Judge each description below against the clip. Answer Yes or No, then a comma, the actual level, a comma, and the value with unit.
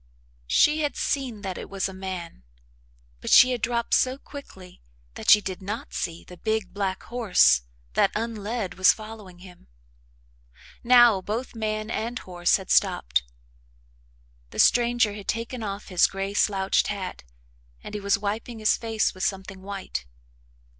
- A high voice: Yes, high, 205 Hz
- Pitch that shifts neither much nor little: Yes, average, 3.4 semitones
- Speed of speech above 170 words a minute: No, average, 155 wpm